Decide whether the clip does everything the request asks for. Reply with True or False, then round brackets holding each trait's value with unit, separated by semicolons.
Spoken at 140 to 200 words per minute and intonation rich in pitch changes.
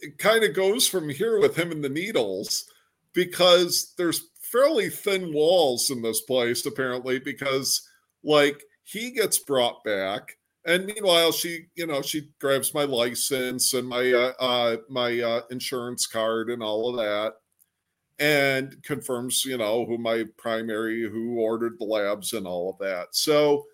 True (160 wpm; 5.9 semitones)